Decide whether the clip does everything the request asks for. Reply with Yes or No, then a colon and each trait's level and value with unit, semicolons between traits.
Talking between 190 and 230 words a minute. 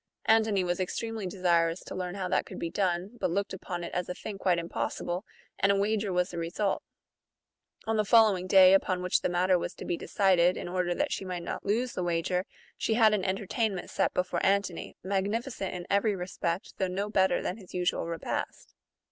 Yes: fast, 205 wpm